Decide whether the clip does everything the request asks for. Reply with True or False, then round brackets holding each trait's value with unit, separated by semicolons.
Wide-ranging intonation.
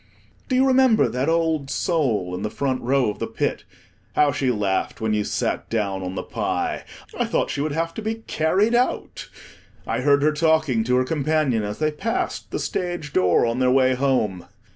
True (6.0 semitones)